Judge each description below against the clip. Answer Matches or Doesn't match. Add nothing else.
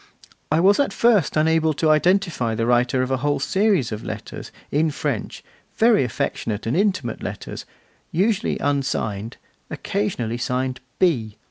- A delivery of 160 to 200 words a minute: Doesn't match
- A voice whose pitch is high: Doesn't match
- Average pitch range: Doesn't match